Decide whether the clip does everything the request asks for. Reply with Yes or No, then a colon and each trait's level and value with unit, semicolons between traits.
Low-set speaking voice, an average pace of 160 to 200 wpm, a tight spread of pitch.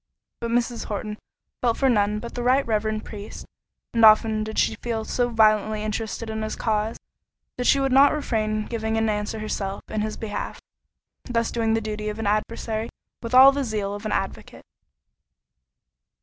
No: high, 220 Hz; average, 175 wpm; narrow, 1.7 semitones